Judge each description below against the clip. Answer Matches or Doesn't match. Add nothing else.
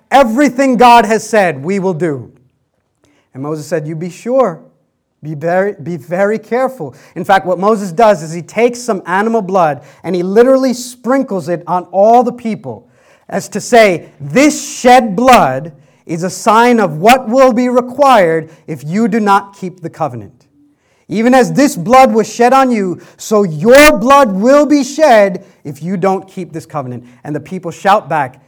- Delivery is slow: Doesn't match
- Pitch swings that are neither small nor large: Doesn't match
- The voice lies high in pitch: Matches